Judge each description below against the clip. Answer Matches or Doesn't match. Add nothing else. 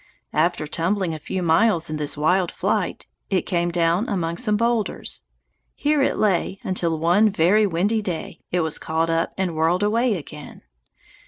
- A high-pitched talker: Doesn't match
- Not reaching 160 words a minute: Doesn't match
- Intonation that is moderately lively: Matches